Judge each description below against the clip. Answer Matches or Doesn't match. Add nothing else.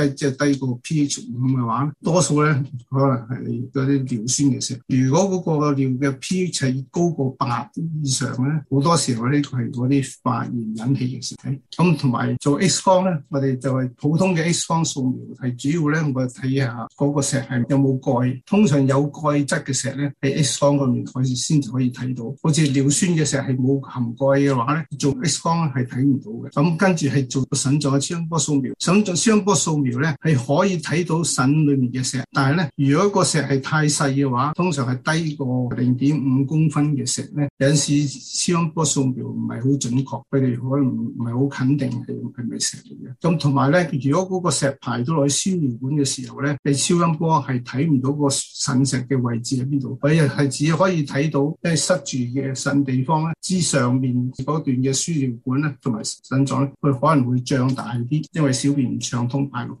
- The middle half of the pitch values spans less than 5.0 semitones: Matches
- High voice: Doesn't match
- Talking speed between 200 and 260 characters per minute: Doesn't match